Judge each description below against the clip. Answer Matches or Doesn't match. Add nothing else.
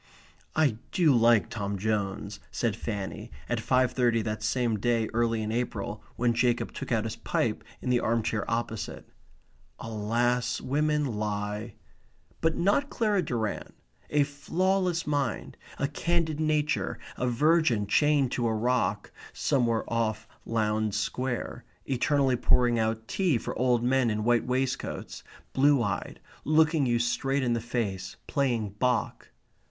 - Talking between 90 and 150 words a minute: Matches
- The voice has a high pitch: Doesn't match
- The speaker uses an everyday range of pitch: Matches